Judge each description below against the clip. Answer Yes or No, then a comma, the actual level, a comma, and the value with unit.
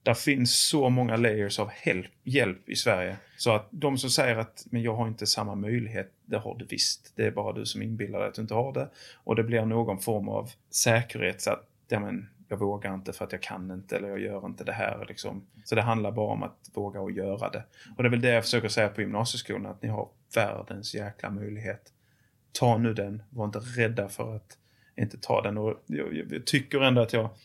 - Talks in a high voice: No, low, 115 Hz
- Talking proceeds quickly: Yes, fast, 235 wpm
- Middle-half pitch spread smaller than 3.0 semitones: Yes, narrow, 2.5 semitones